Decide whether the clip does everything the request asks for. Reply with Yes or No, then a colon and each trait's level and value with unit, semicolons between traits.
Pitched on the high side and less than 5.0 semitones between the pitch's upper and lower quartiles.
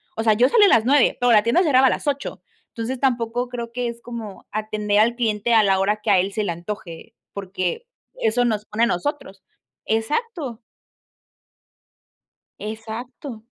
Yes: high, 225 Hz; average, 2.8 semitones